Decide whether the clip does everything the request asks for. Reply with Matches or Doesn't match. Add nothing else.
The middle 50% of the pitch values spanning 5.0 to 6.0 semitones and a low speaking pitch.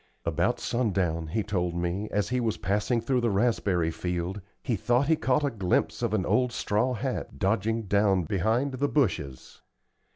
Matches